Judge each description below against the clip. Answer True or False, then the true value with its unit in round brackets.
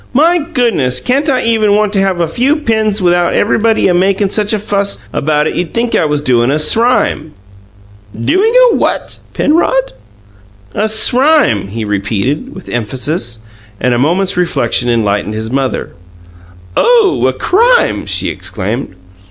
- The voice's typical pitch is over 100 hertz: True (190 Hz)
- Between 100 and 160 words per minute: True (150 wpm)